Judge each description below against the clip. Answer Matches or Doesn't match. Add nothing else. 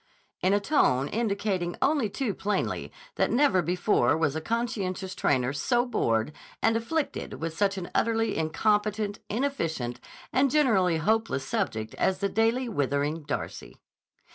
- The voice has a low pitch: Doesn't match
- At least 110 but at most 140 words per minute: Matches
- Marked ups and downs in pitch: Matches